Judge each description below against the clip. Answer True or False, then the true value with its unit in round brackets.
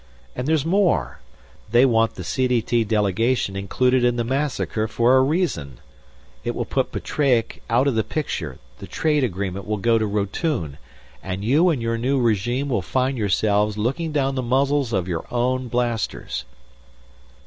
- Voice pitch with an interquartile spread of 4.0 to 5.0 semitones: True (4.3 semitones)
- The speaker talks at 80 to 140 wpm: False (160 wpm)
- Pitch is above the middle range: False (120 Hz)